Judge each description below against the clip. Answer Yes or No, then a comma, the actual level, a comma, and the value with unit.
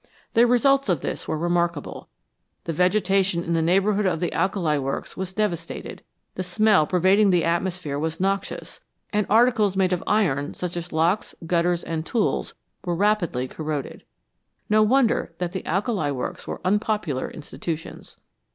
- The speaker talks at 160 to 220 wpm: No, average, 150 wpm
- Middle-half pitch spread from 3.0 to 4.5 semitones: Yes, average, 3.9 semitones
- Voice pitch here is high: No, medium, 180 Hz